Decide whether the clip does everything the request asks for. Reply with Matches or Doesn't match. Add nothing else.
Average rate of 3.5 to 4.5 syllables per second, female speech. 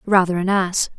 Doesn't match